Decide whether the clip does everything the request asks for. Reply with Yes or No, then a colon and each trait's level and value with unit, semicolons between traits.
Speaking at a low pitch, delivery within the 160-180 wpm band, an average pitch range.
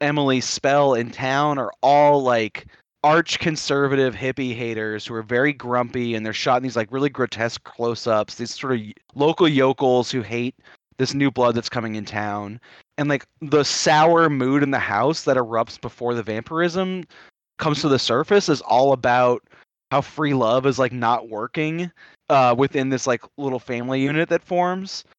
Yes: low, 130 Hz; average, 175 wpm; average, 3.4 semitones